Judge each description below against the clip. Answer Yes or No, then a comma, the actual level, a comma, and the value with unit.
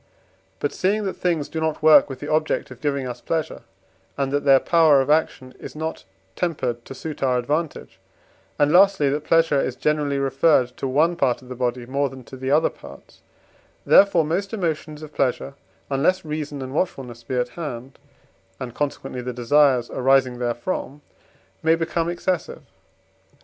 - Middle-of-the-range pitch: Yes, medium, 145 Hz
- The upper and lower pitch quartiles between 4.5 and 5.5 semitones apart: No, average, 3.7 semitones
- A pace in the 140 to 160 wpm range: No, average, 170 wpm